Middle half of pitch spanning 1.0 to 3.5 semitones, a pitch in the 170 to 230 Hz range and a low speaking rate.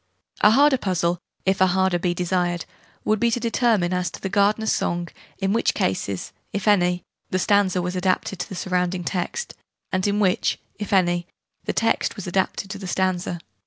No: narrow, 2.4 semitones; medium, 185 Hz; average, 185 wpm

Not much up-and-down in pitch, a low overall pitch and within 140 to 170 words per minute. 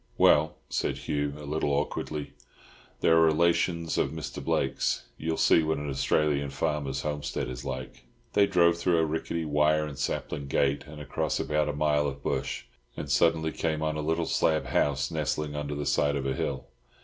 No: narrow, 1.9 semitones; very low, 75 Hz; average, 185 wpm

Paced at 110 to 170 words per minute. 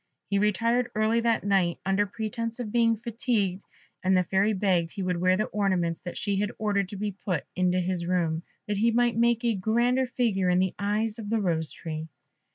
No: fast, 205 wpm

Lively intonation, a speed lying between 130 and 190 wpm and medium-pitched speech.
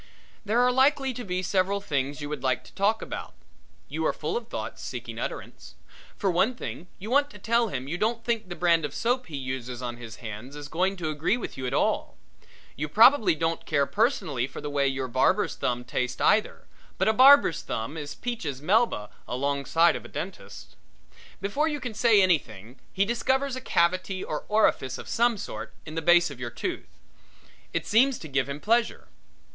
No: wide, 8.5 semitones; average, 200 wpm; medium, 175 Hz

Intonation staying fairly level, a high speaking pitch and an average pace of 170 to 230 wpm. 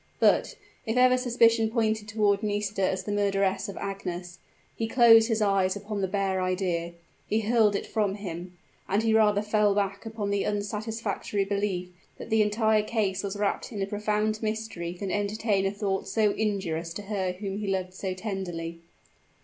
Yes: narrow, 2.1 semitones; high, 205 Hz; average, 175 wpm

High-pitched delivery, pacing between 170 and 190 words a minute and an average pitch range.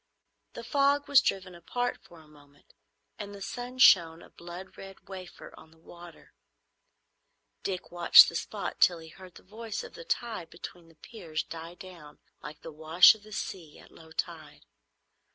No: medium, 175 Hz; average, 175 wpm; average, 4.5 semitones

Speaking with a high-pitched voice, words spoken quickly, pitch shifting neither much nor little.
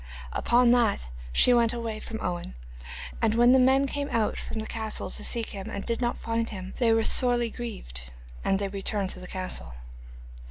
No: high, 225 Hz; average, 195 wpm; average, 3.4 semitones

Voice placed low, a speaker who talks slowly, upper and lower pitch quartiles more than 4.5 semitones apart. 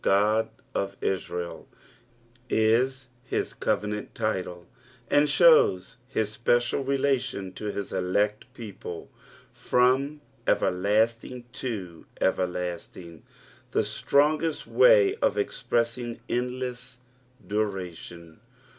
Yes: low, 115 Hz; slow, 95 wpm; average, 5.2 semitones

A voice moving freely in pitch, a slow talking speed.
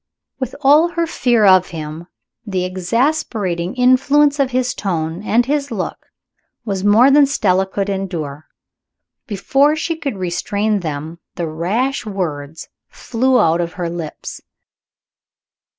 Yes: wide, 7.0 semitones; slow, 130 wpm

